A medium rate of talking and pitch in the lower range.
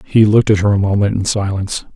No: fast, 245 wpm; low, 100 Hz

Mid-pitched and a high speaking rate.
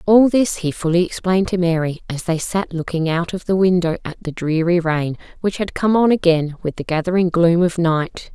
Yes: medium, 175 Hz; fast, 215 wpm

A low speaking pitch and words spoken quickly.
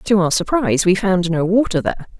No: high, 190 Hz; fast, 220 wpm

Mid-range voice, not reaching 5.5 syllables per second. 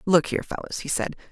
No: medium, 175 Hz; 6.7 syllables/s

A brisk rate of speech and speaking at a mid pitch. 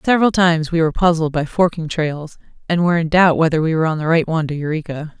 Yes: fast, 240 wpm; medium, 160 Hz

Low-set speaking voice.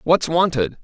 No: medium, 155 Hz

